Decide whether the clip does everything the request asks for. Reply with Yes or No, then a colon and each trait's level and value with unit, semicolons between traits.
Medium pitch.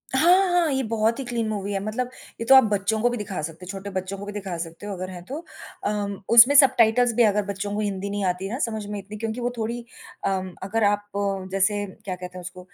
No: high, 205 Hz